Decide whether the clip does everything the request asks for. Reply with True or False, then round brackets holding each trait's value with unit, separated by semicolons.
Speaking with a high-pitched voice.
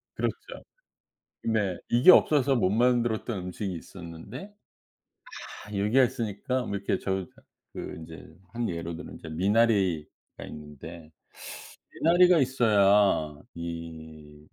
False (100 Hz)